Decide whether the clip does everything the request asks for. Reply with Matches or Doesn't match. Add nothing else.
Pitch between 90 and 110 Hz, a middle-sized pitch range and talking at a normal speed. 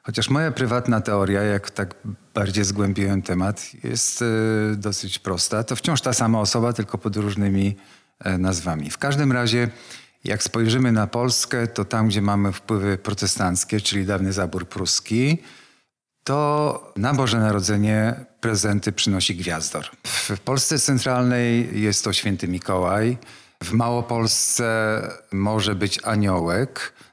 Matches